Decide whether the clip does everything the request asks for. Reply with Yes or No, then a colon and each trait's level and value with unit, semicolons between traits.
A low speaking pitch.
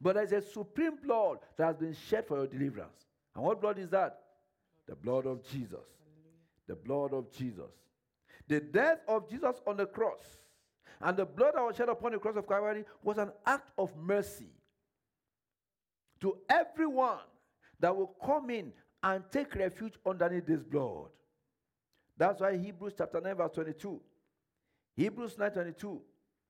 No: high, 195 Hz